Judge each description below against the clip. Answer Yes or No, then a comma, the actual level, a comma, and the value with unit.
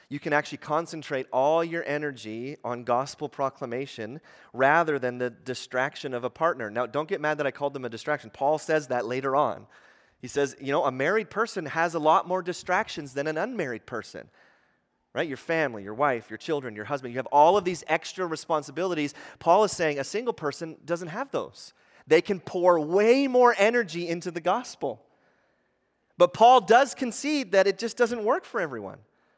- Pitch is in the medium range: Yes, medium, 155 Hz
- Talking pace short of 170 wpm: No, average, 190 wpm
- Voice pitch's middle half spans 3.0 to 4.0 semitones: No, average, 5.2 semitones